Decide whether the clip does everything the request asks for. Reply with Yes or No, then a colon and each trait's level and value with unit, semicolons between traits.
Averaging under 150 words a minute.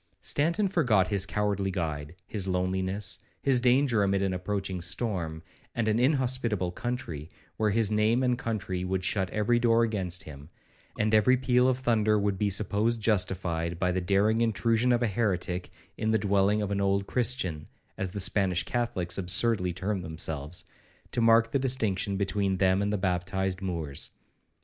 No: average, 165 wpm